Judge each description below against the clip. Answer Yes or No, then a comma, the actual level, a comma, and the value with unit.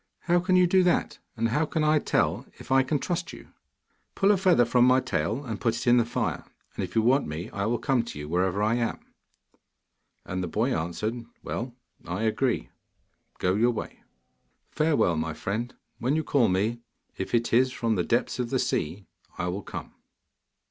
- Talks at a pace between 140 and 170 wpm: No, average, 200 wpm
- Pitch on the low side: Yes, low, 120 Hz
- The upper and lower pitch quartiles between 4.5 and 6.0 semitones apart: Yes, average, 5.1 semitones